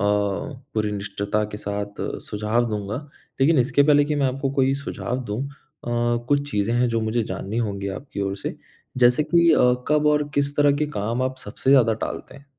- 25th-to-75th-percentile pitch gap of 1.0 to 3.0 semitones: No, wide, 5.4 semitones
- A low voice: Yes, low, 120 Hz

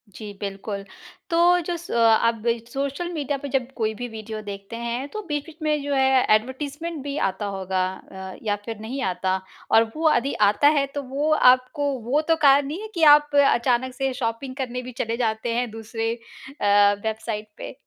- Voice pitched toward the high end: Yes, very high, 250 Hz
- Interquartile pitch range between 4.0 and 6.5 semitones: Yes, average, 4.5 semitones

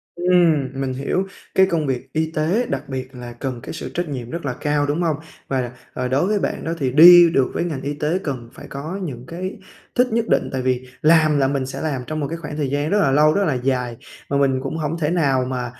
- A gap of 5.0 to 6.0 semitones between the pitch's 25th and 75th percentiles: No, average, 4.2 semitones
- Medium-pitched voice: Yes, medium, 145 Hz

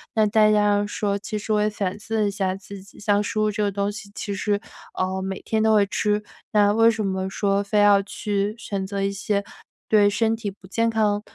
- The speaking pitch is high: Yes, high, 205 Hz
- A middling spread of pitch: No, narrow, 1.2 semitones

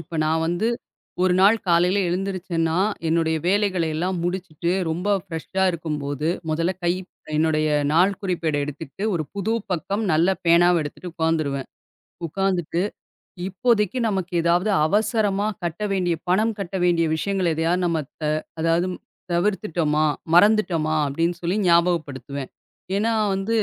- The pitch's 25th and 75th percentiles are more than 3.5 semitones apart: No, average, 3.2 semitones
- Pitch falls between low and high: Yes, medium, 175 Hz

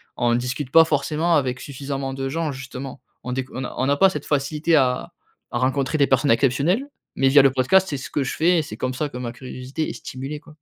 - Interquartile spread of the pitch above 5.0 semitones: No, average, 2.8 semitones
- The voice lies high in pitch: No, low, 135 Hz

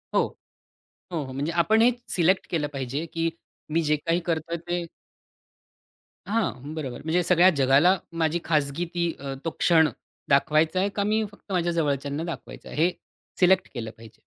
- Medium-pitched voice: Yes, medium, 165 Hz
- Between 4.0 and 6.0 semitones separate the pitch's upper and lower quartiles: No, average, 3.5 semitones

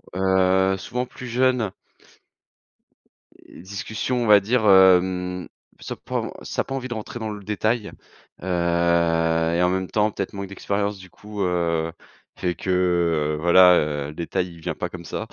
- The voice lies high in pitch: No, very low, 95 Hz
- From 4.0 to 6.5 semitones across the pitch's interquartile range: No, average, 3.0 semitones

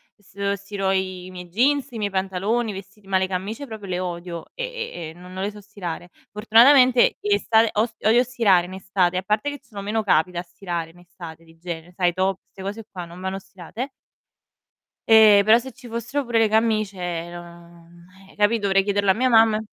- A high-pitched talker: Yes, high, 200 Hz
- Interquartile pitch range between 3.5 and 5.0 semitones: Yes, average, 3.8 semitones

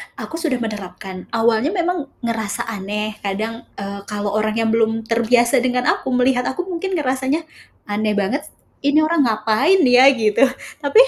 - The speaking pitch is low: No, high, 230 Hz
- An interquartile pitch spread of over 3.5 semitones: Yes, average, 4.2 semitones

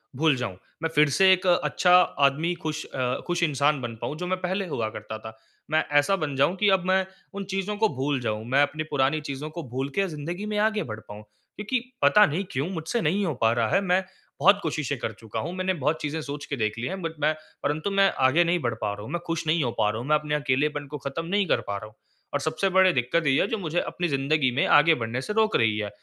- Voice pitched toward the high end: No, medium, 150 Hz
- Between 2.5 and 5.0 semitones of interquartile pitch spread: No, wide, 5.5 semitones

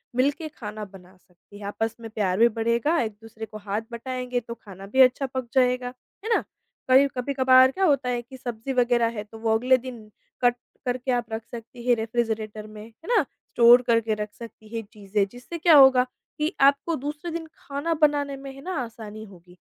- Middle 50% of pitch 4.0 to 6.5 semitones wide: No, average, 3.3 semitones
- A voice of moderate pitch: No, high, 240 Hz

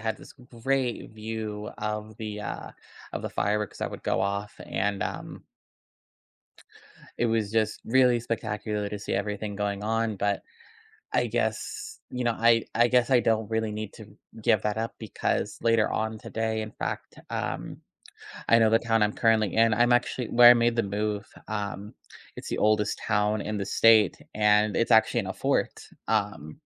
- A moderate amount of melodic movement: No, narrow, 1.6 semitones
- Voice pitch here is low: Yes, low, 110 Hz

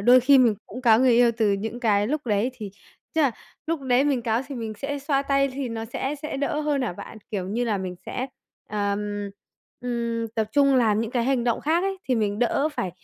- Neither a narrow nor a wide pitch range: Yes, average, 4.1 semitones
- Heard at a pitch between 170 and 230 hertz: No, high, 240 Hz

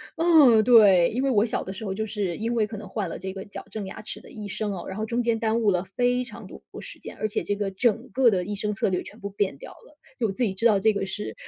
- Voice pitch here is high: Yes, high, 210 Hz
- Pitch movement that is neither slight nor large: Yes, average, 3.0 semitones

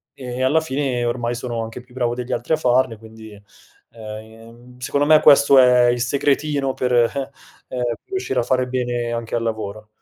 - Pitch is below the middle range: Yes, low, 125 Hz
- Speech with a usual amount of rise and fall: No, narrow, 2.0 semitones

